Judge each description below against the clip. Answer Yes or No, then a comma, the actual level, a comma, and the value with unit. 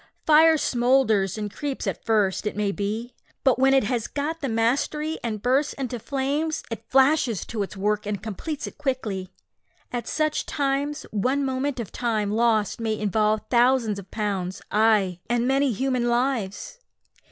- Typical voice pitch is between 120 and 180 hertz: No, high, 240 Hz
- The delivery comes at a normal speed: Yes, average, 165 wpm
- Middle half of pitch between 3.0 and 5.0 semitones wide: Yes, average, 4.3 semitones